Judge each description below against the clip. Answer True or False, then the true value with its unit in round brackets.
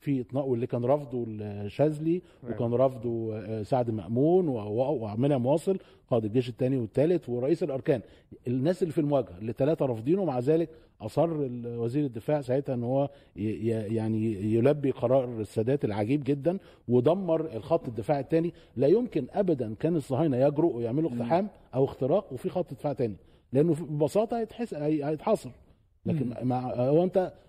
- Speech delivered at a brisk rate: True (140 wpm)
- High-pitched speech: False (135 Hz)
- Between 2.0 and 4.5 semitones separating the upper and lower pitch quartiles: False (5.2 semitones)